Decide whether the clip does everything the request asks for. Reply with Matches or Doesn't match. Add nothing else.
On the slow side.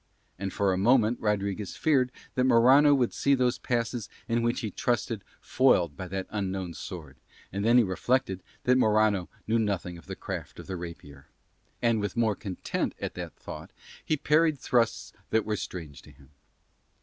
Doesn't match